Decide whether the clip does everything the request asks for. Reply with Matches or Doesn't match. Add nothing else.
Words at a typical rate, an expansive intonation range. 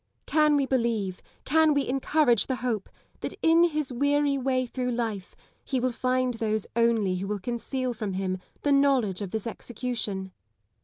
Doesn't match